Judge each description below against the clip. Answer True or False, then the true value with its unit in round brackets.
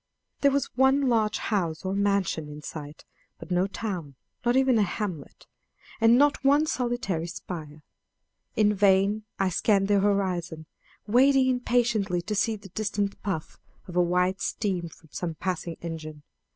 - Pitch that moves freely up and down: False (4.7 semitones)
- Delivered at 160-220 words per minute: False (150 wpm)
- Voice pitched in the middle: False (195 Hz)